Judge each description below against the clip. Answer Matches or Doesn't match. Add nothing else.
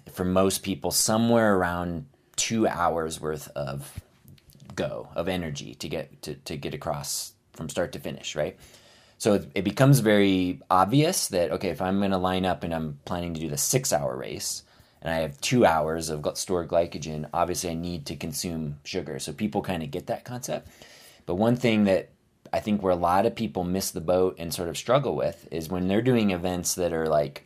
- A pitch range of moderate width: Matches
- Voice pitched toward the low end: Matches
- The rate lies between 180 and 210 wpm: Matches